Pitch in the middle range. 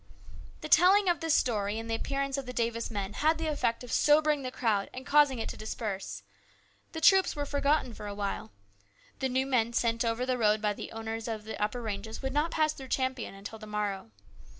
No: high, 235 Hz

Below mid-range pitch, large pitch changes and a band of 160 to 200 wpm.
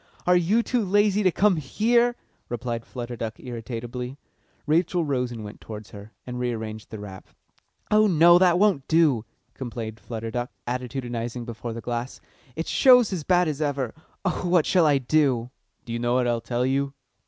Yes: low, 130 Hz; wide, 6.7 semitones; average, 175 wpm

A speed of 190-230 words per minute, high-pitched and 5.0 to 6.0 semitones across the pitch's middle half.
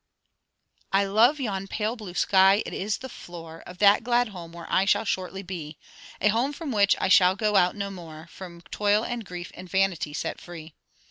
No: average, 200 wpm; high, 195 Hz; average, 3.2 semitones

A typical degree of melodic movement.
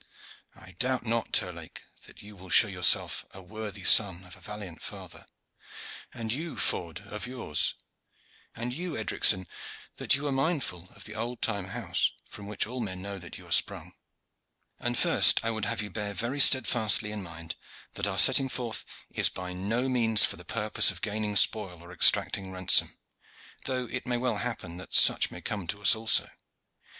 Yes: average, 4.3 semitones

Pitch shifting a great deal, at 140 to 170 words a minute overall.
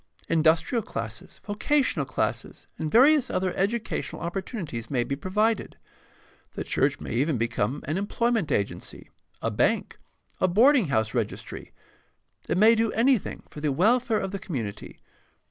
Yes: wide, 8.6 semitones; average, 145 wpm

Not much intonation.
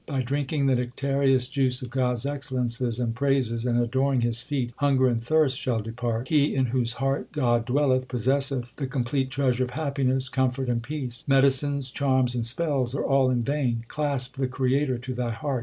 Yes: narrow, 2.1 semitones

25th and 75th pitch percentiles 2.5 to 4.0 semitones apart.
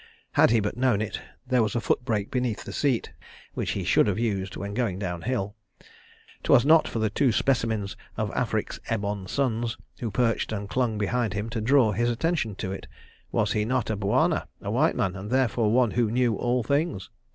Yes: average, 3.3 semitones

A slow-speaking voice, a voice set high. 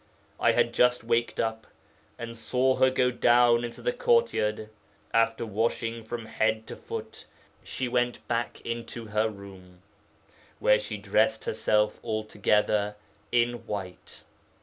No: slow, 130 wpm; low, 115 Hz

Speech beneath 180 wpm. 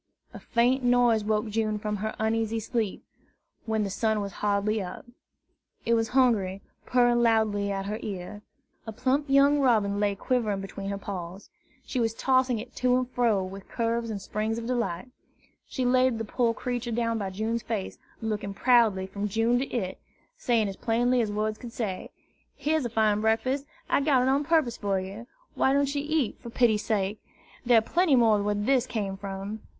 No: average, 185 wpm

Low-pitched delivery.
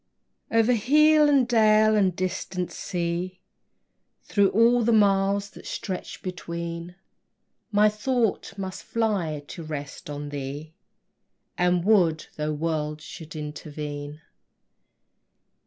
No: medium, 185 Hz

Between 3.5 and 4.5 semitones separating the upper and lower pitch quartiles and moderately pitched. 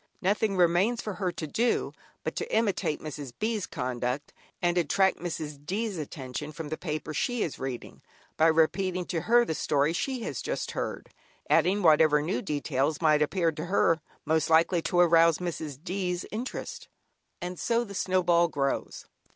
Yes: average, 4.0 semitones; medium, 170 Hz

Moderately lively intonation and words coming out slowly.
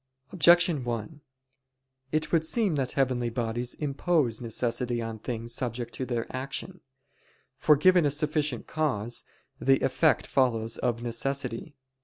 Yes: average, 4.4 semitones; slow, 130 wpm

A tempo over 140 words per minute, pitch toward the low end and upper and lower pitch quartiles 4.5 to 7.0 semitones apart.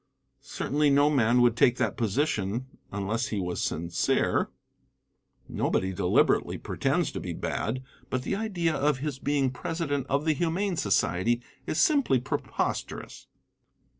No: slow, 135 wpm; low, 130 Hz; wide, 5.5 semitones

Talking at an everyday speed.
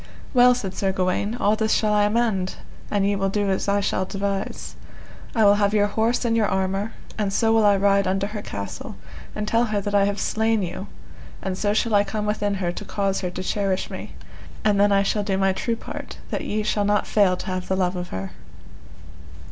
No: fast, 225 wpm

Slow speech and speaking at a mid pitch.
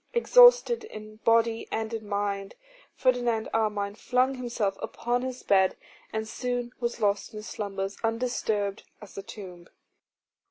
No: slow, 130 wpm; high, 220 Hz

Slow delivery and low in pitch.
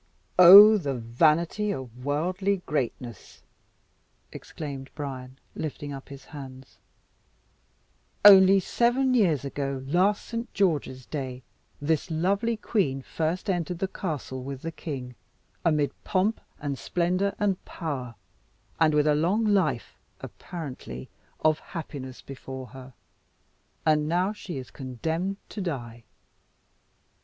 No: slow, 115 wpm; medium, 155 Hz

